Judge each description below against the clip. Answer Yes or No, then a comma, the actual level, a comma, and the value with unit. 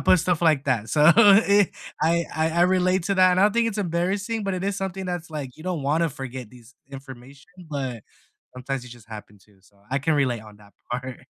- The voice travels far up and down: Yes, wide, 6.4 semitones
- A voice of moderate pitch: Yes, medium, 155 Hz